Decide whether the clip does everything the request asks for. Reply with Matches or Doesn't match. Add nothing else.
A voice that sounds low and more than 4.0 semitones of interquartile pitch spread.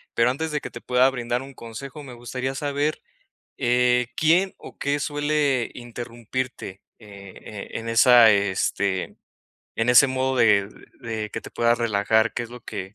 Doesn't match